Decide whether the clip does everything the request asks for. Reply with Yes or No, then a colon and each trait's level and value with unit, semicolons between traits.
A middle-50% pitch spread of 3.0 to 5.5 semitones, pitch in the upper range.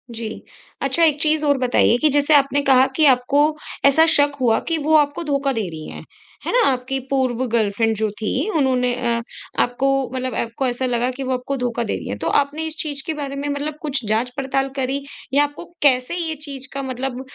No: narrow, 2.6 semitones; very high, 270 Hz